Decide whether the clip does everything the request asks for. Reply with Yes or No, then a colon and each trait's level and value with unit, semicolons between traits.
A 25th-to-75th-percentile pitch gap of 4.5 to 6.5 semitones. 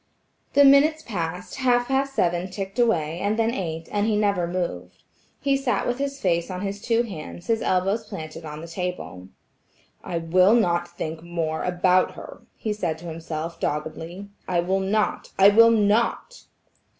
Yes: average, 5.1 semitones